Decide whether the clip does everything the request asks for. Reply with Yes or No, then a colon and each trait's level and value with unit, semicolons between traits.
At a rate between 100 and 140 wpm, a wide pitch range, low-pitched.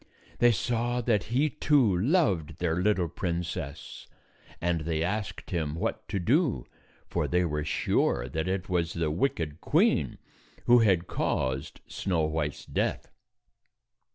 Yes: slow, 135 wpm; wide, 5.9 semitones; very low, 90 Hz